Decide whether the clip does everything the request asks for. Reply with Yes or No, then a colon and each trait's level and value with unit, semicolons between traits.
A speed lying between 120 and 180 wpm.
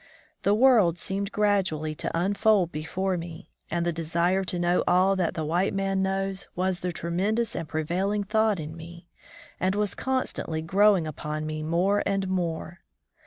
Yes: average, 165 wpm